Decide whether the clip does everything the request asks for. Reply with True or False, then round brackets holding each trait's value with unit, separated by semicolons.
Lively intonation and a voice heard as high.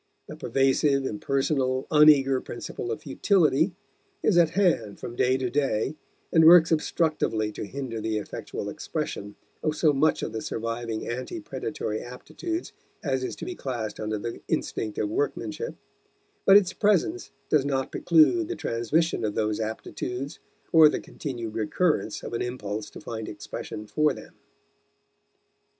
False (6.0 semitones; 135 Hz)